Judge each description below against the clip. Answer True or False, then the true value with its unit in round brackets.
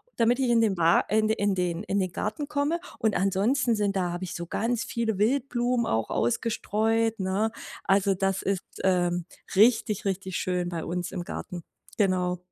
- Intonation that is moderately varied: True (3.9 semitones)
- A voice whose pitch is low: False (200 Hz)